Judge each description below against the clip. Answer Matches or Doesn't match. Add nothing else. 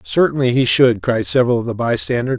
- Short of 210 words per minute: Matches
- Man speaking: Matches